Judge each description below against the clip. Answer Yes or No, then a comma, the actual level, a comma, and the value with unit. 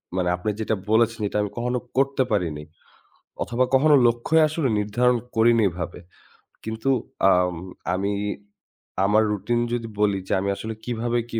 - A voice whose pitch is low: Yes, low, 110 Hz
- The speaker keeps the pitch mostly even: No, average, 3.3 semitones